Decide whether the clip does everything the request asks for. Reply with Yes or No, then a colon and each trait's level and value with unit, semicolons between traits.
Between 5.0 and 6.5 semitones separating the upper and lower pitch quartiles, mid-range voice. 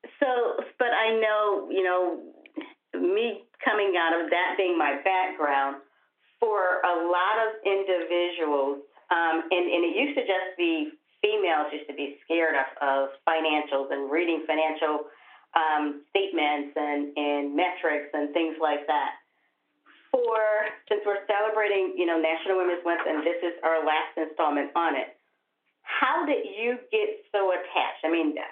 Yes: wide, 5.5 semitones; medium, 175 Hz